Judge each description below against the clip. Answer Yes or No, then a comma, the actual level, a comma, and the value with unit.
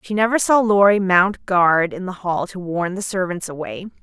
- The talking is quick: Yes, fast, 210 wpm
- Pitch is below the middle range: No, high, 190 Hz